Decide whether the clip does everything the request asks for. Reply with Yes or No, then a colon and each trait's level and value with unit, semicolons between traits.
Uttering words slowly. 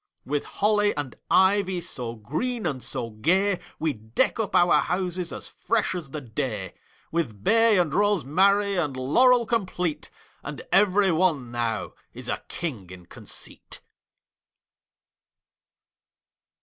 Yes: slow, 125 wpm